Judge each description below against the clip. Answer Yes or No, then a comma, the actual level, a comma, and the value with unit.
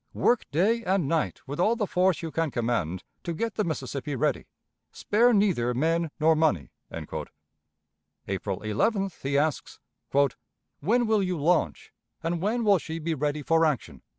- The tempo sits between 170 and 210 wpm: No, average, 155 wpm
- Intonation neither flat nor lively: No, wide, 5.7 semitones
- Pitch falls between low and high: Yes, medium, 160 Hz